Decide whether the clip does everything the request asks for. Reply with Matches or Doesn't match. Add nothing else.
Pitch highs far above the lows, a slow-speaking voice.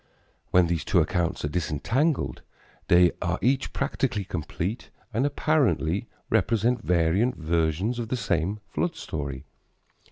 Matches